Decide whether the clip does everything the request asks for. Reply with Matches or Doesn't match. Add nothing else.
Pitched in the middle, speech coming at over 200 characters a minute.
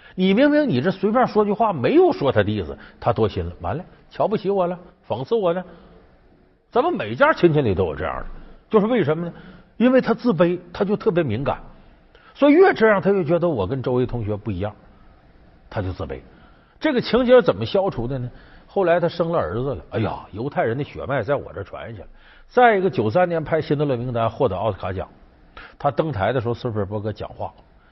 Matches